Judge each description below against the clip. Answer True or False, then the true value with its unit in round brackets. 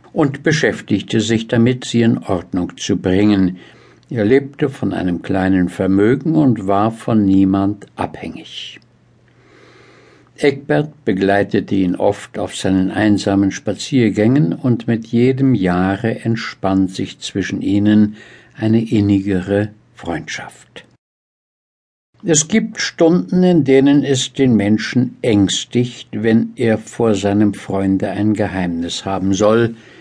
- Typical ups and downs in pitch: True (4.1 semitones)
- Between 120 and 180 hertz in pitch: False (105 Hz)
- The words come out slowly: True (115 wpm)